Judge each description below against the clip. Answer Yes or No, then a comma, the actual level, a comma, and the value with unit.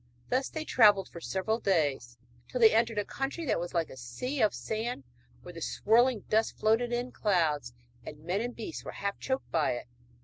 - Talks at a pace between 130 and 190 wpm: No, average, 200 wpm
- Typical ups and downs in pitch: No, wide, 6.3 semitones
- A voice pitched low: No, high, 210 Hz